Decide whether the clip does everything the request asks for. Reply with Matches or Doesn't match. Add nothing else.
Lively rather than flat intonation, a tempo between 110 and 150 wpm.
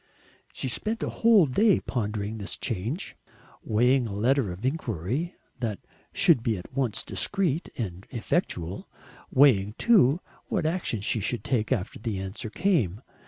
Matches